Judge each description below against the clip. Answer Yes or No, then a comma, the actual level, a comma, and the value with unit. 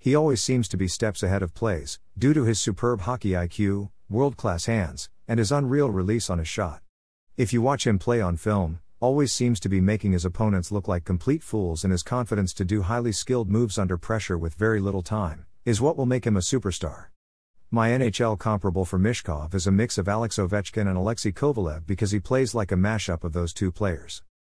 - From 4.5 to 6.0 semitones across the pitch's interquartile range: No, average, 4.1 semitones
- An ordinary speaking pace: No, fast, 215 wpm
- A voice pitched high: No, low, 105 Hz